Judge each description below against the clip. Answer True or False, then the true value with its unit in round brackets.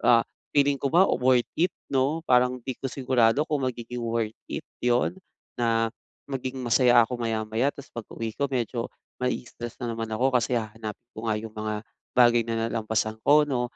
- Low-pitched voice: True (120 Hz)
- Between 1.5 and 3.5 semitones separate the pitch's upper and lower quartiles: True (2.5 semitones)